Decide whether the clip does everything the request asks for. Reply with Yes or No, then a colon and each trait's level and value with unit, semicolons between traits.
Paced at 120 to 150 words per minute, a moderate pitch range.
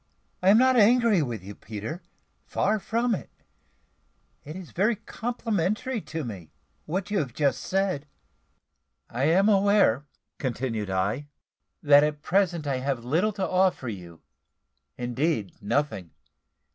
No: slow, 135 wpm; wide, 8.3 semitones